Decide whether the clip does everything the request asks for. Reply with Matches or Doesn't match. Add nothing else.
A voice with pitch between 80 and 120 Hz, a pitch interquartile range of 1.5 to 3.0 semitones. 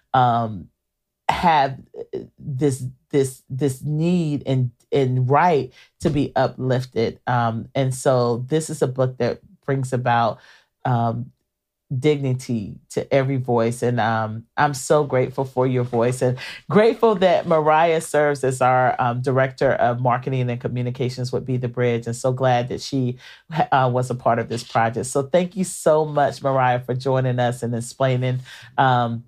Doesn't match